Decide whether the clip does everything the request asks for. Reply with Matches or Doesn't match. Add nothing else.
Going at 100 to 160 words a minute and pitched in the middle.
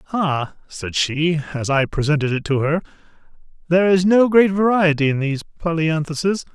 Matches